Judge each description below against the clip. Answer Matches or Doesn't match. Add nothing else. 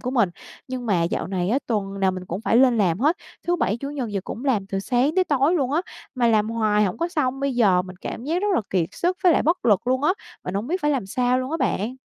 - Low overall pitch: Doesn't match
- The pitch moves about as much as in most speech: Doesn't match